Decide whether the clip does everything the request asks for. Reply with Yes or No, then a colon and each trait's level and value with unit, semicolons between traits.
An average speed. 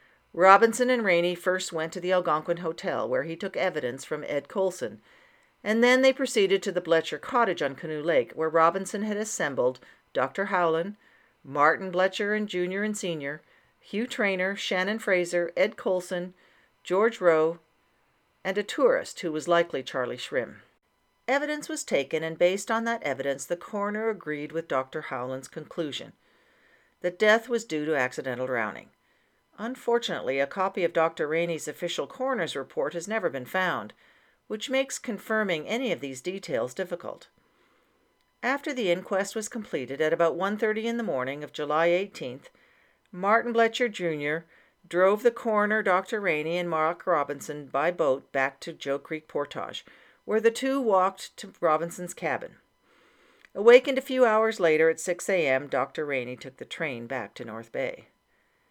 Yes: average, 160 wpm